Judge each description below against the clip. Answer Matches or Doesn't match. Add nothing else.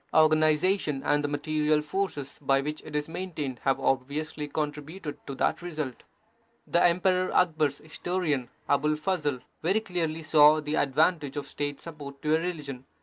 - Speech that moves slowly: Doesn't match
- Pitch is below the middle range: Doesn't match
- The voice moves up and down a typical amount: Doesn't match